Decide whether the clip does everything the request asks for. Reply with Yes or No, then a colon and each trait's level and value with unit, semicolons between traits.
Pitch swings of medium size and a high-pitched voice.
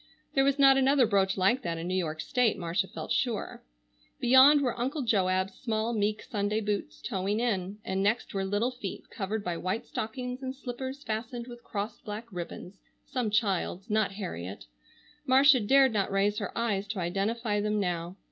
Yes: average, 4.2 semitones; high, 210 Hz